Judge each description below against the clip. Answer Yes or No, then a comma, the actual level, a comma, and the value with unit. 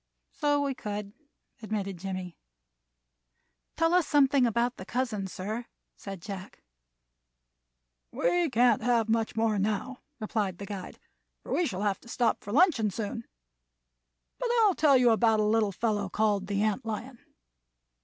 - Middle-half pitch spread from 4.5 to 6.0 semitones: No, average, 3.7 semitones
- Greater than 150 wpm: No, average, 145 wpm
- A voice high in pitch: Yes, high, 220 Hz